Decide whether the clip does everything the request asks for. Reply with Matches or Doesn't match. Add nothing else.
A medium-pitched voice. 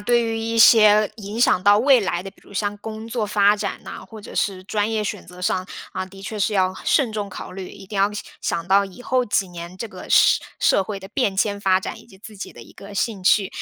Doesn't match